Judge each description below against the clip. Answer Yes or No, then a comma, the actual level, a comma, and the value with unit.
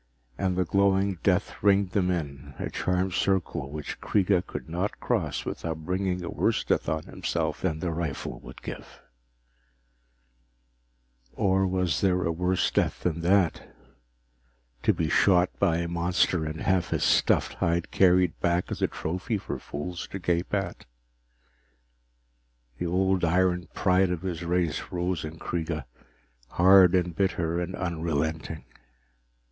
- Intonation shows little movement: Yes, narrow, 2.1 semitones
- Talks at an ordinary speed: Yes, average, 145 wpm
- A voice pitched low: Yes, very low, 90 Hz